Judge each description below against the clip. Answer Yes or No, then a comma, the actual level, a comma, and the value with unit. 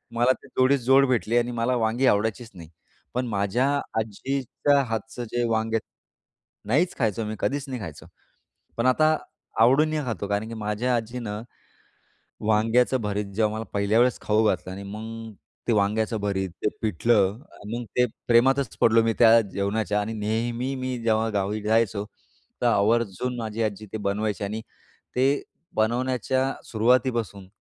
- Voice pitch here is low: Yes, low, 115 Hz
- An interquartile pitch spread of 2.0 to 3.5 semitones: Yes, average, 2.9 semitones